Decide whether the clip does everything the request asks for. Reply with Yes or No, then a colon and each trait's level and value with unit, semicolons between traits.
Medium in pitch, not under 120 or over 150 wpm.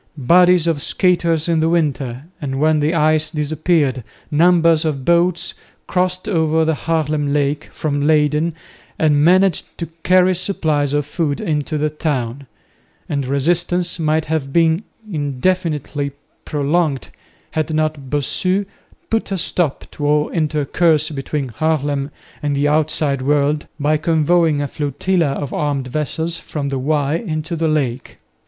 Yes: medium, 155 Hz; average, 140 wpm